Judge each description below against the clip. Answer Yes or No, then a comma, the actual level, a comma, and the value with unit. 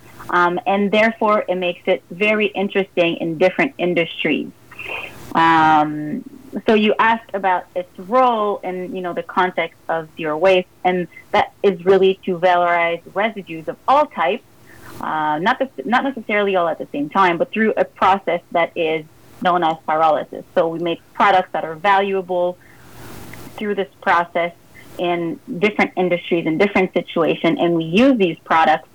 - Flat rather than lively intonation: No, average, 3.1 semitones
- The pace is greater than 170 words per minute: No, average, 160 wpm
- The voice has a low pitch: No, medium, 180 Hz